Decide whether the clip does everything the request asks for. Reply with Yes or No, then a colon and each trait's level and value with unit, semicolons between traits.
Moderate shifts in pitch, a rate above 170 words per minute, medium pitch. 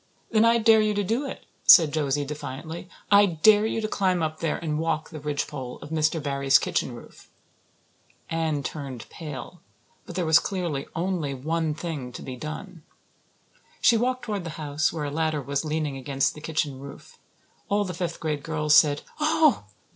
Yes: average, 4.2 semitones; average, 180 wpm; medium, 160 Hz